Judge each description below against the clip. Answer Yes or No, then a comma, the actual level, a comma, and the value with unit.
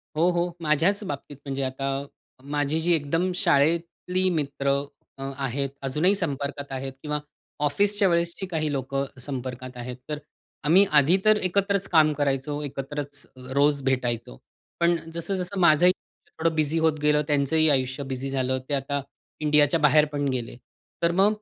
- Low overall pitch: No, medium, 150 Hz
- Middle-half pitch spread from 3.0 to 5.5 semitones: Yes, average, 3.6 semitones